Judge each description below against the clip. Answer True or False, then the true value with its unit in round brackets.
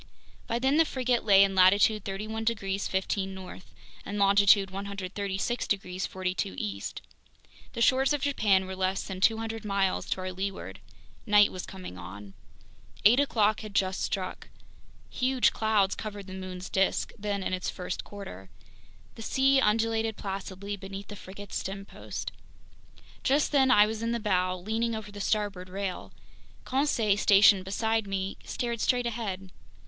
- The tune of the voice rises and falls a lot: False (2.8 semitones)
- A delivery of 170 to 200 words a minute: False (155 wpm)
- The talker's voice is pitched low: False (200 Hz)